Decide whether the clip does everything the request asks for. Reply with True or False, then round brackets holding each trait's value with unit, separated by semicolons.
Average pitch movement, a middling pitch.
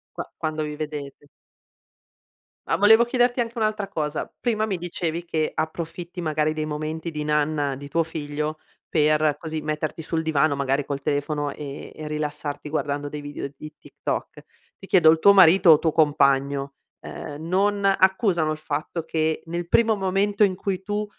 True (3.7 semitones; 155 Hz)